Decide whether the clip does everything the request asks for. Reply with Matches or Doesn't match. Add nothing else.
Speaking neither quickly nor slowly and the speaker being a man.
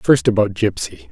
Matches